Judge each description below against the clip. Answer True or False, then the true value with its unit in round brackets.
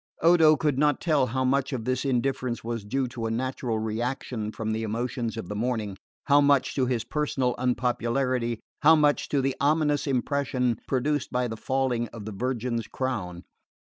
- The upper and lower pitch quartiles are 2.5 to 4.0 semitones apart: True (3.0 semitones)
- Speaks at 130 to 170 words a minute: False (180 wpm)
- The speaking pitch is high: False (125 Hz)